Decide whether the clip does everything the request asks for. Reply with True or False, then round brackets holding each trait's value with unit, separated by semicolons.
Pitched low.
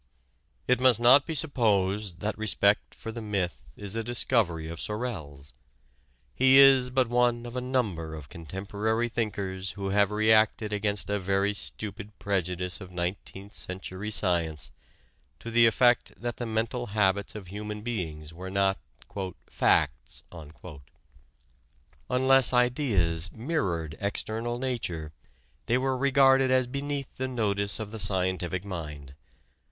True (105 Hz)